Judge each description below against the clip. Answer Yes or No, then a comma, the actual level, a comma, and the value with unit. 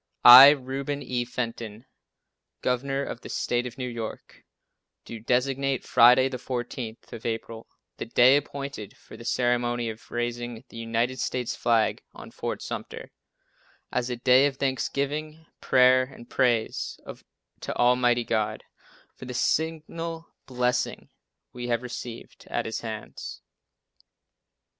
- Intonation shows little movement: Yes, narrow, 2.1 semitones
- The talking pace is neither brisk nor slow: No, slow, 130 wpm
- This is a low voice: Yes, low, 125 Hz